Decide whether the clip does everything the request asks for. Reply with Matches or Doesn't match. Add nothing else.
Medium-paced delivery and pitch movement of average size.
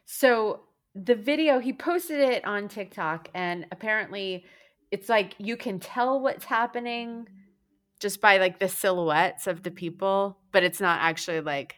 Matches